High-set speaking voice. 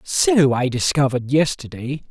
No: medium, 140 Hz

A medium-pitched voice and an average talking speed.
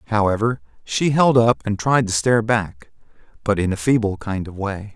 No: low, 110 Hz; average, 195 wpm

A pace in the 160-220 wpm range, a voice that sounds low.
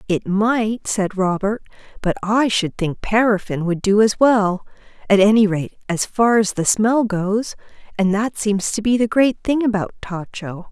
No: average, 175 wpm; high, 205 Hz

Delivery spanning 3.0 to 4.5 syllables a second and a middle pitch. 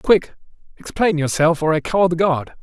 No: 4.8 syllables/s; medium, 170 Hz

